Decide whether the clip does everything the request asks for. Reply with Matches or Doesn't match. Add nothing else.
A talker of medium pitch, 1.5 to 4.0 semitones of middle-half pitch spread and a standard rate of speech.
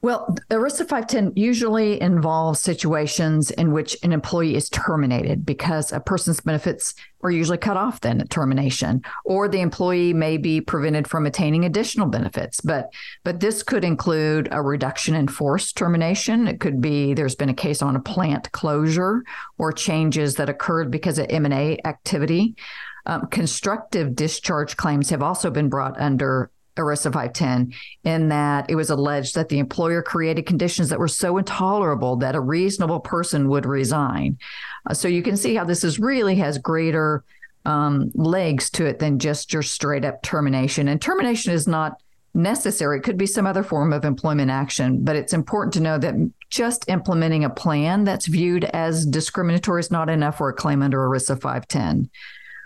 Matches